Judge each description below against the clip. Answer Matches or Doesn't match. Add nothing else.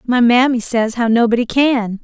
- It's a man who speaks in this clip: Doesn't match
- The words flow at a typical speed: Matches